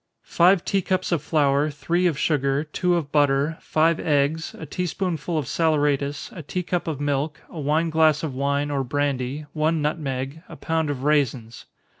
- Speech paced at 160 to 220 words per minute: Yes, average, 185 wpm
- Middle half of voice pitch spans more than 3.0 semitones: No, narrow, 2.5 semitones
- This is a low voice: No, medium, 150 Hz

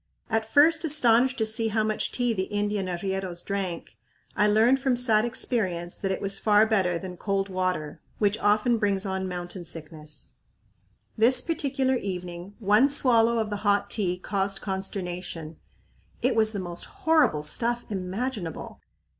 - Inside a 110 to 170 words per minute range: Yes, average, 155 wpm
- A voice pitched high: Yes, high, 205 Hz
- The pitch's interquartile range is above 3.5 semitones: Yes, average, 3.9 semitones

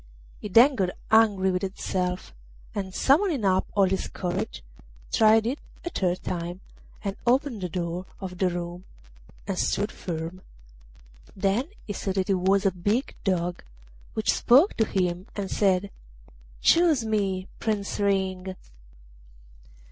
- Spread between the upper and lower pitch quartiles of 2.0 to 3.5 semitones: Yes, average, 2.8 semitones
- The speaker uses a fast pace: No, average, 140 wpm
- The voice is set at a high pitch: Yes, high, 195 Hz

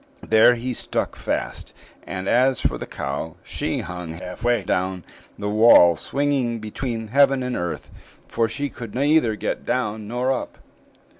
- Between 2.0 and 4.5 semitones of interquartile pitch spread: No, average, 5.2 semitones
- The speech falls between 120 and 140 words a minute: No, average, 155 wpm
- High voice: No, low, 115 Hz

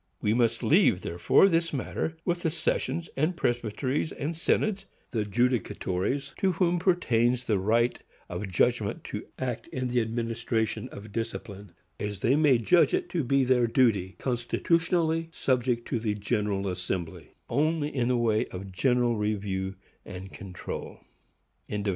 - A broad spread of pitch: Yes, wide, 6.0 semitones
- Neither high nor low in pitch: No, low, 120 Hz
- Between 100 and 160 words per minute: Yes, average, 140 wpm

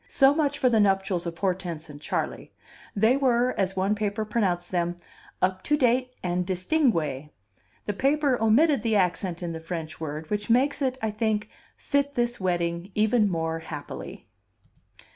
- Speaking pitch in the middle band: No, high, 200 Hz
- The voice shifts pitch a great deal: Yes, wide, 5.9 semitones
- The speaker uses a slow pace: No, average, 160 wpm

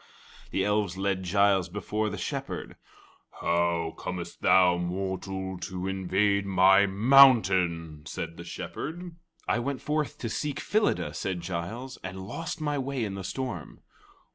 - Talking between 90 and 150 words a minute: Yes, average, 140 wpm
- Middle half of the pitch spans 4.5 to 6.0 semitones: Yes, average, 4.8 semitones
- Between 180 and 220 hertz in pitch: No, very low, 95 Hz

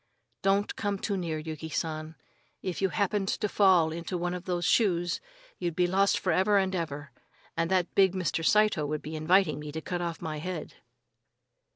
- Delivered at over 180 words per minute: Yes, average, 190 wpm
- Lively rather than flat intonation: No, average, 3.2 semitones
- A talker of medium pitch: Yes, medium, 175 Hz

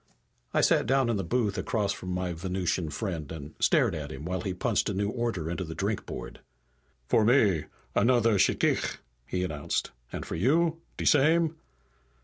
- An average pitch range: No, wide, 5.9 semitones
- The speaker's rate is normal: Yes, average, 170 wpm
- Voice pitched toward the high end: No, very low, 95 Hz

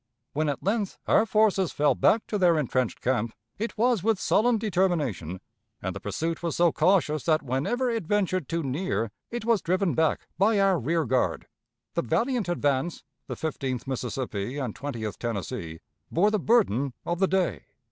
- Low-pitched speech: No, medium, 165 Hz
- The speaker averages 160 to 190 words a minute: Yes, average, 170 wpm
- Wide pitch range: Yes, wide, 7.4 semitones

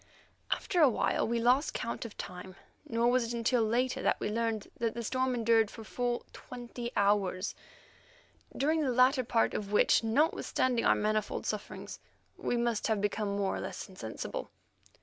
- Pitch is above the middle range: Yes, high, 230 Hz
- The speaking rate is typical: Yes, average, 170 wpm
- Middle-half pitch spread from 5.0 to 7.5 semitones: No, average, 2.7 semitones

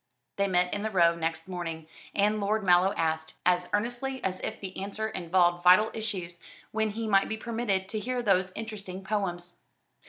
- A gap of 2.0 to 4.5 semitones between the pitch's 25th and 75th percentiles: Yes, average, 3.4 semitones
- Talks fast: No, average, 180 wpm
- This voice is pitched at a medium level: No, high, 195 Hz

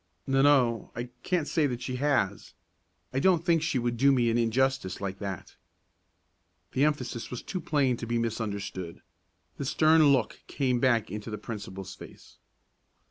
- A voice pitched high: No, low, 125 Hz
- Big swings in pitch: No, average, 4.1 semitones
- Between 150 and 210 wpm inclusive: Yes, average, 165 wpm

